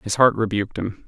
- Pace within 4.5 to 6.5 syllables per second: Yes, 5.8 syllables/s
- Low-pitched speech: Yes, low, 105 Hz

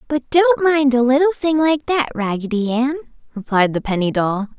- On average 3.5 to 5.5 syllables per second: Yes, 4.9 syllables/s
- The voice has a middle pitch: No, very high, 255 Hz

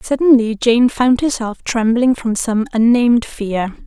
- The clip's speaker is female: Yes, female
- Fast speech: No, average, 140 wpm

